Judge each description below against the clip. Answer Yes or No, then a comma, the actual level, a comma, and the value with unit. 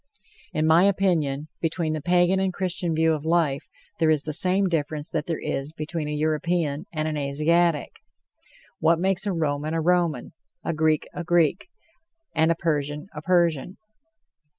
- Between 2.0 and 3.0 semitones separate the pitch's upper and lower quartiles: Yes, narrow, 2.4 semitones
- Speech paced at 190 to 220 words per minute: No, average, 165 wpm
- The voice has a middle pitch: Yes, medium, 160 Hz